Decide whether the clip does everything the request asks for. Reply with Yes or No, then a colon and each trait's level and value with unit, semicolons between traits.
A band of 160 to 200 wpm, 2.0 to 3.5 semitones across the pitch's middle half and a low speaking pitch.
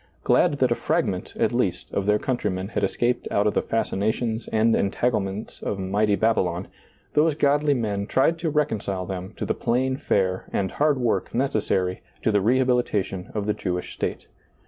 No: average, 180 wpm; average, 4.4 semitones; low, 110 Hz